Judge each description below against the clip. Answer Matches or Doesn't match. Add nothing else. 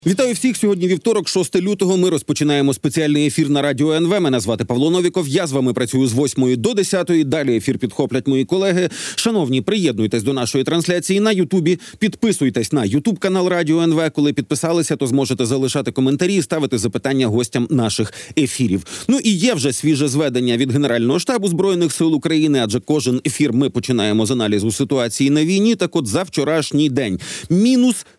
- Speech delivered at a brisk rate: Matches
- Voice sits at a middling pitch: Matches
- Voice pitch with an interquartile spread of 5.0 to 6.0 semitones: Matches